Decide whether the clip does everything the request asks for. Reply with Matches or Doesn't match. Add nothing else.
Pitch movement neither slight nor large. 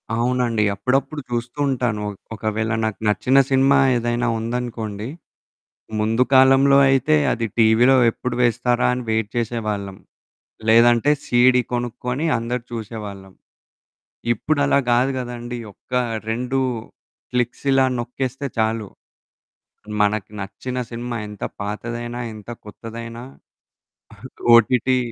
Doesn't match